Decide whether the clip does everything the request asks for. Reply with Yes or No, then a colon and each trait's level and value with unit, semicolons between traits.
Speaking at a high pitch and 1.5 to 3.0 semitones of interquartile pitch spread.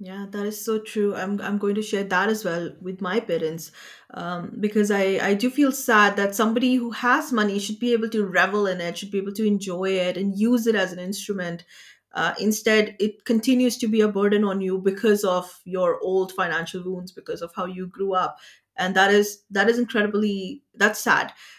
Yes: high, 205 Hz; narrow, 2.5 semitones